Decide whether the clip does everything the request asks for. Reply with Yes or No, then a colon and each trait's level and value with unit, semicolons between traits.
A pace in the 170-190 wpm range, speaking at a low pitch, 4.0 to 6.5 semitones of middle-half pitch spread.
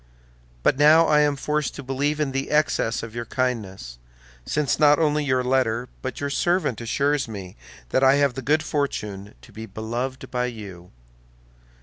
Yes: average, 175 wpm; low, 130 Hz; average, 4.5 semitones